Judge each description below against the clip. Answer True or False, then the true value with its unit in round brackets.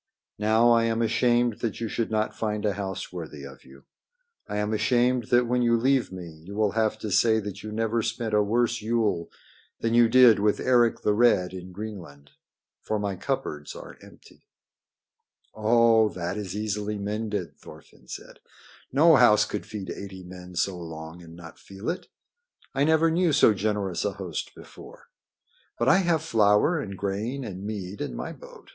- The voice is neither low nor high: False (105 Hz)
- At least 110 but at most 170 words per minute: False (180 wpm)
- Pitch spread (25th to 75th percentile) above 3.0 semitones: True (3.6 semitones)